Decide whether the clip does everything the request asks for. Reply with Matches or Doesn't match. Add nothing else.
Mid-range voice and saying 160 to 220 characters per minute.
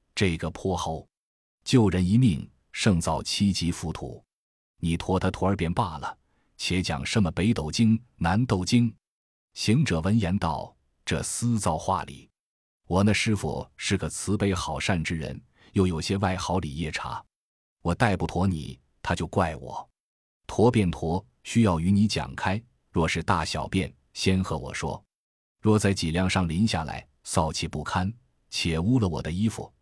Doesn't match